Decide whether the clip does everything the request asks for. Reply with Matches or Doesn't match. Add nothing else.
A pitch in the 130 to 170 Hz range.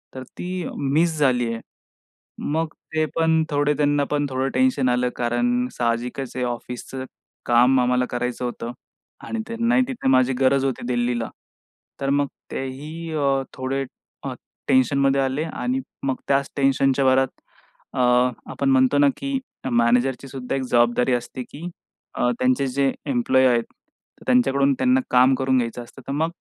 Matches